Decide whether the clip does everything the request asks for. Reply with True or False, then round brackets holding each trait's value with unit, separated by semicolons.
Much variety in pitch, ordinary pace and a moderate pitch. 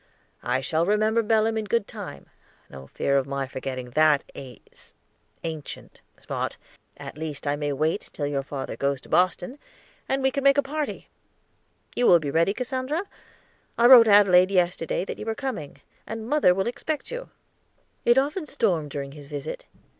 True (8.7 semitones; 170 wpm; 180 Hz)